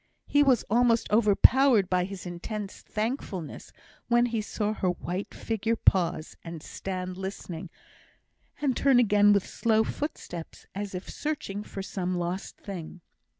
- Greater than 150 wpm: No, average, 140 wpm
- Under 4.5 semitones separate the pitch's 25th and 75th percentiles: Yes, average, 4.1 semitones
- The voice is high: Yes, high, 205 Hz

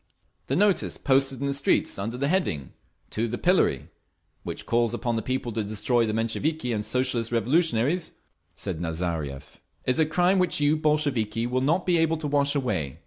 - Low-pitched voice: Yes, low, 130 Hz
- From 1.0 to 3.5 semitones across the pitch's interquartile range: No, wide, 5.5 semitones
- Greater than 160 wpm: Yes, average, 180 wpm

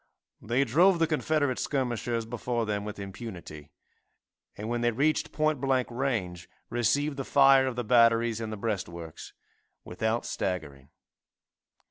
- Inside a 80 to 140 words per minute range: Yes, slow, 135 wpm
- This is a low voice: Yes, low, 120 Hz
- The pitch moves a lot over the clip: No, average, 4.7 semitones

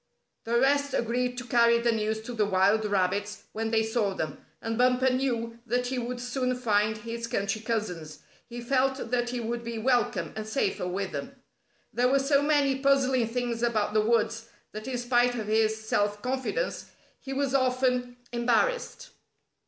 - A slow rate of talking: No, average, 175 wpm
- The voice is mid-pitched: No, high, 235 Hz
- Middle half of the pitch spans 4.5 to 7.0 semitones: No, narrow, 2.6 semitones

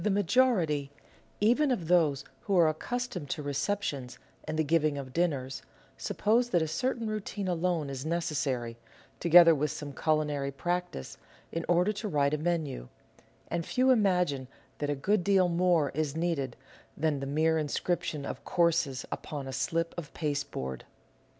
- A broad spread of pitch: No, average, 4.0 semitones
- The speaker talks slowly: No, average, 165 wpm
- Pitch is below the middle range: No, medium, 160 Hz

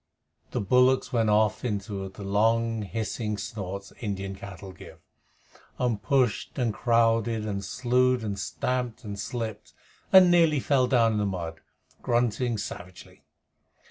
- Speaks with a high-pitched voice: No, low, 110 Hz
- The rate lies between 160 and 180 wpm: No, average, 140 wpm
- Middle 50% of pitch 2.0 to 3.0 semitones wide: No, average, 3.7 semitones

